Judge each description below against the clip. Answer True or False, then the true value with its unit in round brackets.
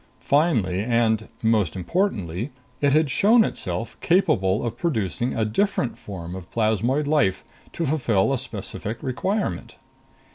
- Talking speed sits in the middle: False (130 wpm)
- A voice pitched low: True (115 Hz)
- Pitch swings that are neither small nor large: False (7.6 semitones)